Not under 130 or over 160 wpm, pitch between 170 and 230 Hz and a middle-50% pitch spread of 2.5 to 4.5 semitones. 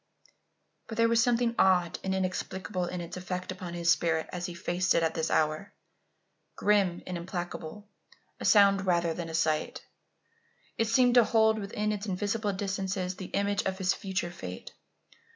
No: average, 170 wpm; high, 190 Hz; average, 2.9 semitones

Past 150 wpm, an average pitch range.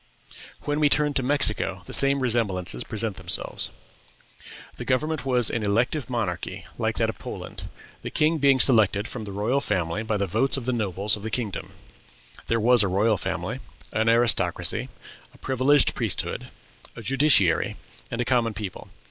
Yes: average, 165 wpm; average, 4.5 semitones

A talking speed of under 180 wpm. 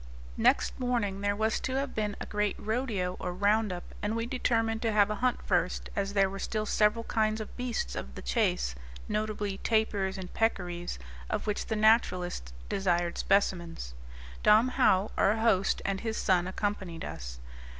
Yes: average, 170 wpm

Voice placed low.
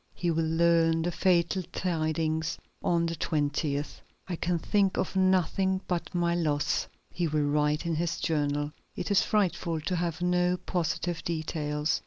No: medium, 165 Hz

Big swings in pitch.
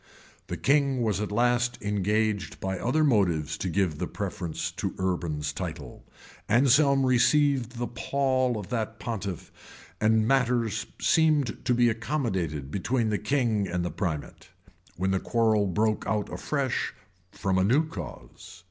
No: average, 4.8 semitones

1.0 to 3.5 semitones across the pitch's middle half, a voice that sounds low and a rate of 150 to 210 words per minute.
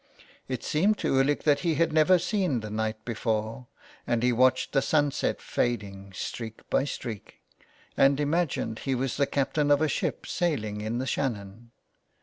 No: average, 4.8 semitones; low, 130 Hz; average, 165 wpm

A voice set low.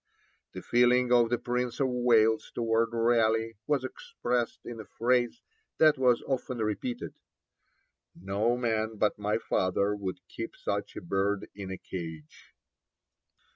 Yes: low, 115 Hz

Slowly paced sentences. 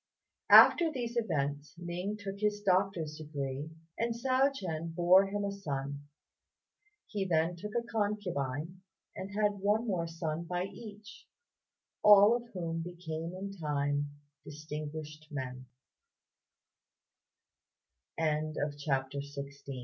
Yes: slow, 105 wpm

